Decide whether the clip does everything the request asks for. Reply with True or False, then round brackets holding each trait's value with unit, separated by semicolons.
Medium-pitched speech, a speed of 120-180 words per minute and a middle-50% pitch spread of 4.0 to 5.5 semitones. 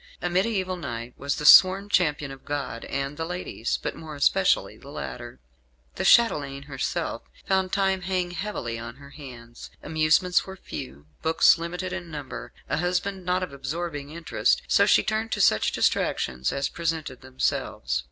True (160 Hz; 160 wpm; 5.0 semitones)